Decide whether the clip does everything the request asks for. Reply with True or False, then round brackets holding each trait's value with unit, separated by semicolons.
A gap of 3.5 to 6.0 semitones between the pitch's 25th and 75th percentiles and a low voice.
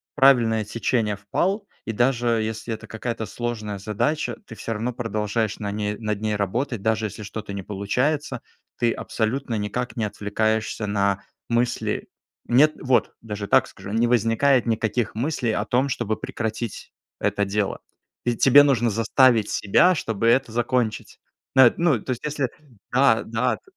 False (2.8 semitones; 115 Hz)